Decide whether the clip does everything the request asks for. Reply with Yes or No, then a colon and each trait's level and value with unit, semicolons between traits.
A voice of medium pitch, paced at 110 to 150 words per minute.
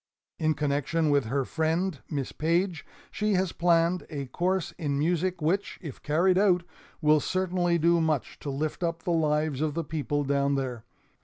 No: medium, 160 Hz; average, 170 wpm